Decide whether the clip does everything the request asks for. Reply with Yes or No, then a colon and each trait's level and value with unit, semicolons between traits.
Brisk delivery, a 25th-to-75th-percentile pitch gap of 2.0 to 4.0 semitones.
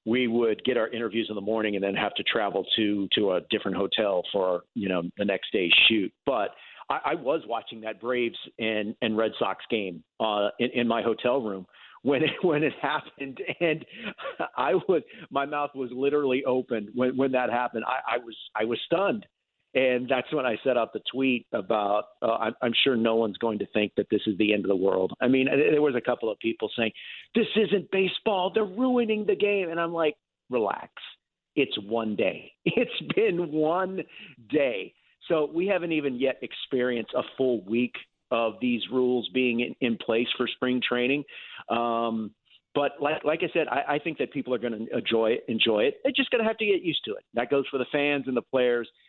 No: fast, 210 wpm; average, 4.8 semitones